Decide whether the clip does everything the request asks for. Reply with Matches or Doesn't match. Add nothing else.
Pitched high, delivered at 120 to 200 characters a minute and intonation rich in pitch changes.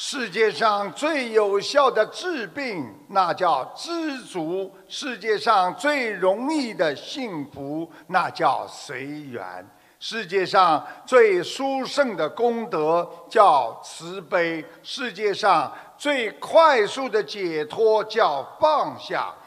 Matches